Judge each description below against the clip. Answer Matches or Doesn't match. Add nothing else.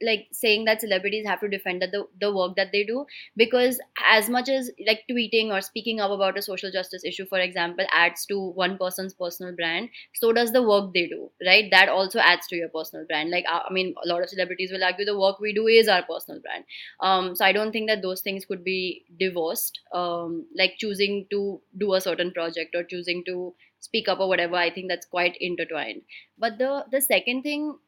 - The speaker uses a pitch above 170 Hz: Matches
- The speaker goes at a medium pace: Doesn't match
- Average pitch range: Matches